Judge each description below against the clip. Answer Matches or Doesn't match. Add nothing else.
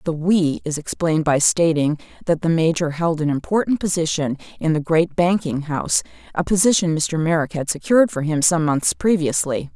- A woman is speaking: Matches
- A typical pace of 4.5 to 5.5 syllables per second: Matches